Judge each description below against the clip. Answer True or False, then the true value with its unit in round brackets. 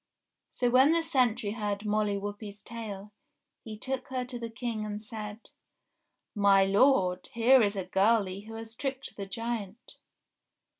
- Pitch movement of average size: True (3.0 semitones)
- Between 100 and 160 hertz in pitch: False (215 Hz)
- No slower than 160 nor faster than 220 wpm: False (150 wpm)